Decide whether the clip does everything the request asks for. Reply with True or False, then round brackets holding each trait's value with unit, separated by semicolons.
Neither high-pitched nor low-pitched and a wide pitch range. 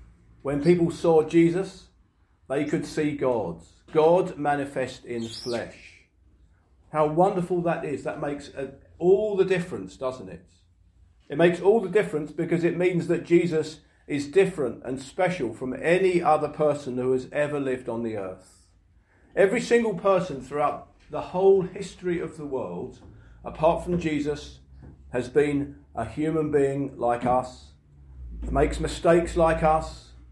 True (145 Hz; 9.0 semitones)